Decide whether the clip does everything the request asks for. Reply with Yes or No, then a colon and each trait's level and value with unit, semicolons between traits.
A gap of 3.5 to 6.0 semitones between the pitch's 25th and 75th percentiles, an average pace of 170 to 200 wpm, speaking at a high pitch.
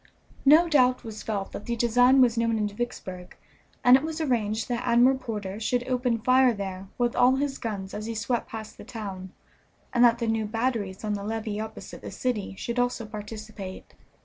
No: average, 2.9 semitones; average, 195 wpm; high, 230 Hz